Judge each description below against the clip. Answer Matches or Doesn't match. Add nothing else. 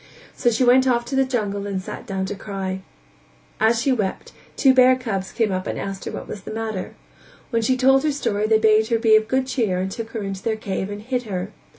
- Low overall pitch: Doesn't match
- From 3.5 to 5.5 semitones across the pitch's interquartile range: Matches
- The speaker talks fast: Matches